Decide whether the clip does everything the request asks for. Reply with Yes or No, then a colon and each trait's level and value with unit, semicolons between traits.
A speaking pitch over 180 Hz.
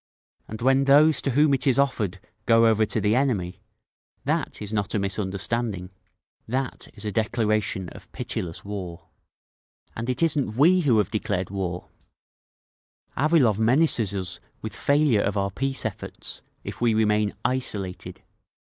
No: low, 110 Hz